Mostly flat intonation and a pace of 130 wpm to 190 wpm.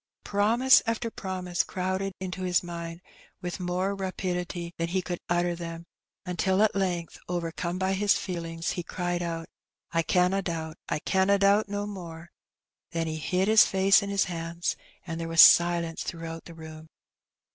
Yes: narrow, 2.3 semitones; average, 170 wpm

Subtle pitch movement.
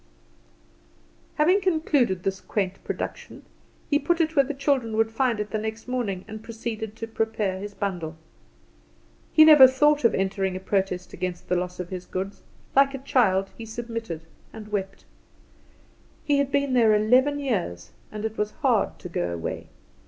No: wide, 5.6 semitones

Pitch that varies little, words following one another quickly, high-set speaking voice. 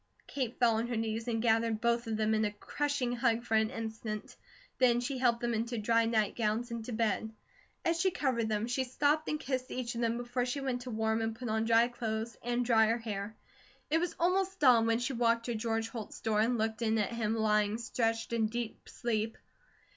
Yes: narrow, 1.7 semitones; fast, 220 wpm; high, 230 Hz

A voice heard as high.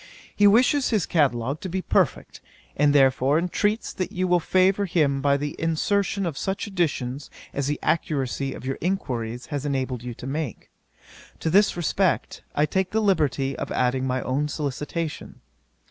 No: medium, 150 Hz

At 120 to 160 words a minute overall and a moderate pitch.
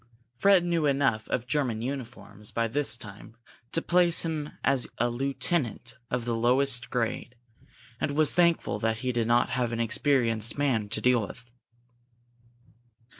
No: average, 150 wpm; low, 125 Hz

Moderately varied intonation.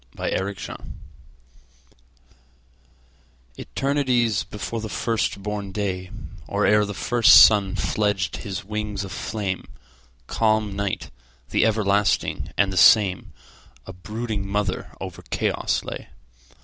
No: narrow, 2.2 semitones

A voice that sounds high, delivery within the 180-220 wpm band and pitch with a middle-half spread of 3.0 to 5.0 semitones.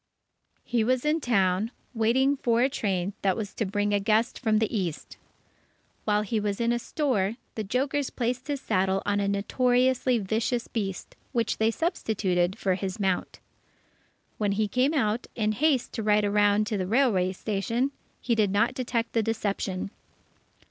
No: high, 220 Hz; average, 170 wpm; average, 3.5 semitones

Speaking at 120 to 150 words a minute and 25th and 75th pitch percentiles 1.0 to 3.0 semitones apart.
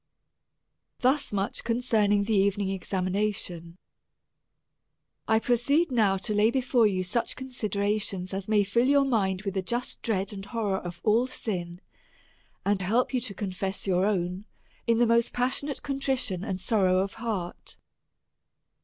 No: average, 145 wpm; average, 3.8 semitones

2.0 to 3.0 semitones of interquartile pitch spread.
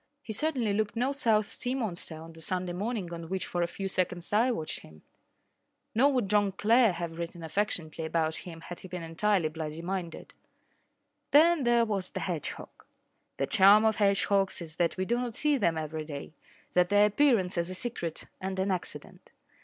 No: average, 4.5 semitones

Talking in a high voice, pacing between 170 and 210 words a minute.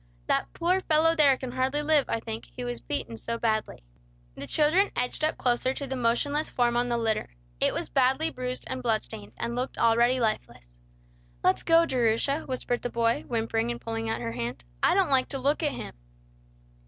Yes: high, 245 Hz; average, 200 wpm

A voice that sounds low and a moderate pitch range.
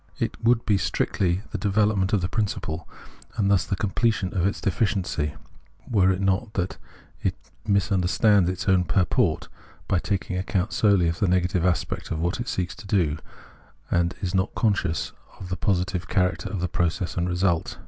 No: very low, 95 Hz; narrow, 2.3 semitones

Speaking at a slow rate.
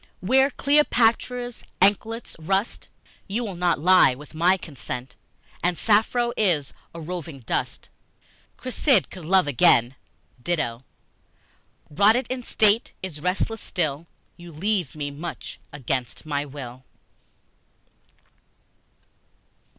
Yes: slow, 105 wpm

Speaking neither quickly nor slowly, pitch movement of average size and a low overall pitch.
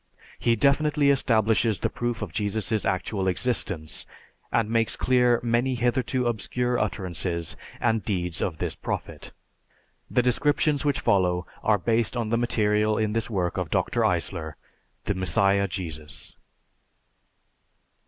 No: slow, 130 wpm; average, 4.2 semitones; low, 110 Hz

